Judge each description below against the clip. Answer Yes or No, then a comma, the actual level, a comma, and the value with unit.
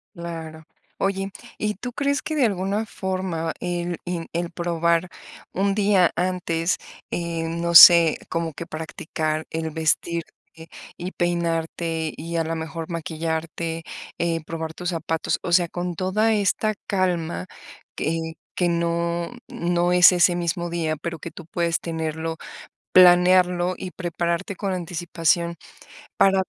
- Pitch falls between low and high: Yes, medium, 170 Hz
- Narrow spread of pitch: Yes, narrow, 1.7 semitones